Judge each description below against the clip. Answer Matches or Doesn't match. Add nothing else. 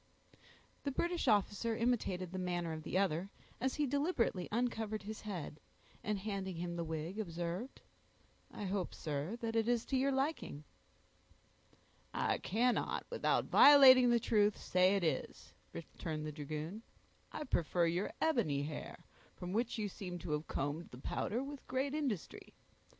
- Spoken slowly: Doesn't match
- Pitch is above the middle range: Matches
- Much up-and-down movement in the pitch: Matches